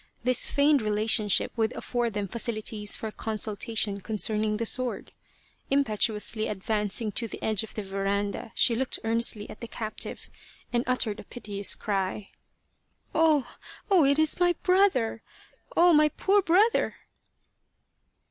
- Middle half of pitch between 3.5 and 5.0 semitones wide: Yes, average, 3.9 semitones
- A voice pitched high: Yes, high, 225 Hz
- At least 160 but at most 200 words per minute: No, average, 140 wpm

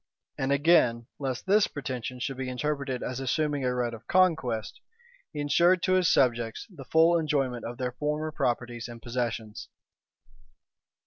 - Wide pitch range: No, average, 4.1 semitones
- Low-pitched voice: Yes, low, 130 Hz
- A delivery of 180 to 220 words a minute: No, average, 150 wpm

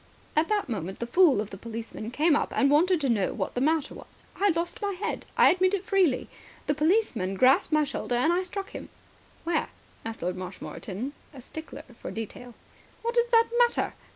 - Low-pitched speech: No, very high, 300 Hz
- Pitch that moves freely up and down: Yes, wide, 8.1 semitones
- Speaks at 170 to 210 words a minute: Yes, average, 200 wpm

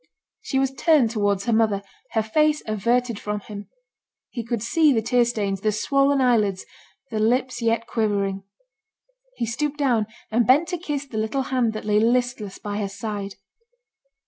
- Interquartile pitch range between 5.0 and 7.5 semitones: No, average, 3.6 semitones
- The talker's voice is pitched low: No, high, 230 Hz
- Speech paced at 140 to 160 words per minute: No, average, 170 wpm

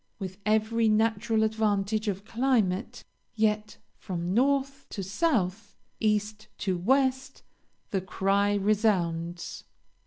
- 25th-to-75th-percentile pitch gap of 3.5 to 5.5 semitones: No, narrow, 2.6 semitones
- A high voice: Yes, high, 215 Hz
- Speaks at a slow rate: Yes, slow, 100 wpm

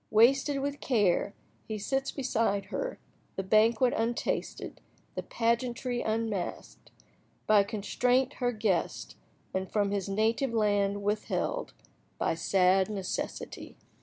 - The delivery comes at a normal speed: No, slow, 105 wpm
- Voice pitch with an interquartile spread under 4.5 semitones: Yes, average, 3.5 semitones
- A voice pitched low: No, high, 220 Hz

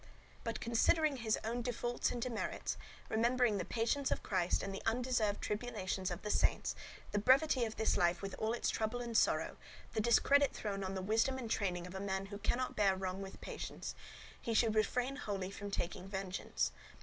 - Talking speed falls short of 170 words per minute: No, average, 195 wpm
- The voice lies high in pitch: Yes, high, 220 Hz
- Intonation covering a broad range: No, average, 3.7 semitones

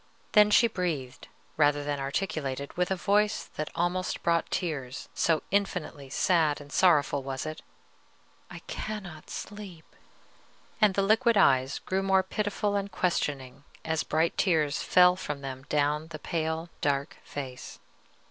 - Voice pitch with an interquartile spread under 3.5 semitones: No, average, 4.9 semitones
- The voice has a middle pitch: Yes, medium, 160 Hz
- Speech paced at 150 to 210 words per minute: No, average, 140 wpm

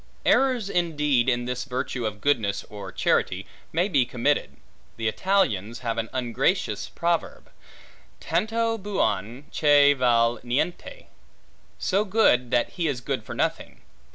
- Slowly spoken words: Yes, slow, 130 wpm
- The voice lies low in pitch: Yes, low, 130 Hz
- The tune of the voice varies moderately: No, wide, 7.1 semitones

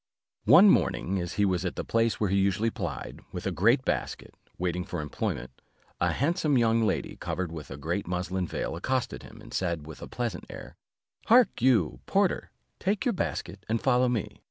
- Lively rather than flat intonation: Yes, wide, 6.0 semitones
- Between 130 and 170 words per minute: No, average, 190 wpm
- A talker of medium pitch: No, low, 100 Hz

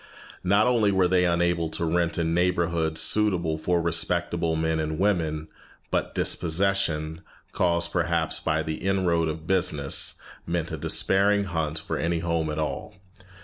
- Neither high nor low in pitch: No, very low, 85 Hz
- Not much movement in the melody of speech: Yes, narrow, 2.0 semitones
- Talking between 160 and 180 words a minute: No, average, 145 wpm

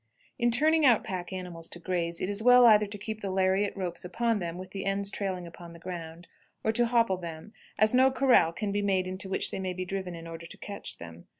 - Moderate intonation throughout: Yes, average, 3.7 semitones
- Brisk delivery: Yes, fast, 240 wpm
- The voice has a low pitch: No, high, 190 Hz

